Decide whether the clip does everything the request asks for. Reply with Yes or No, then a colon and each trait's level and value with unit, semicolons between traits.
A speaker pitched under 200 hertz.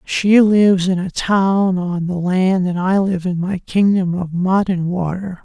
Yes: medium, 185 Hz